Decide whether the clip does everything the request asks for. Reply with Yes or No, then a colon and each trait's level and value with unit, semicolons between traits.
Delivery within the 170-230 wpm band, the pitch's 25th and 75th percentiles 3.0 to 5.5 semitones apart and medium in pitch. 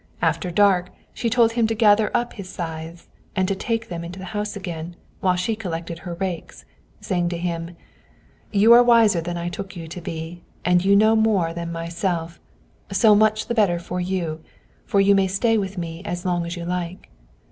Yes: average, 195 wpm; average, 3.4 semitones; medium, 180 Hz